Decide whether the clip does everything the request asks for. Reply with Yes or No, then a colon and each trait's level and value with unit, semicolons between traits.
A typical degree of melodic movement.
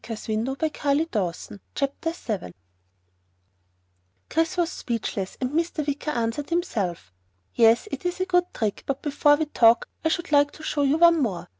No: wide, 6.2 semitones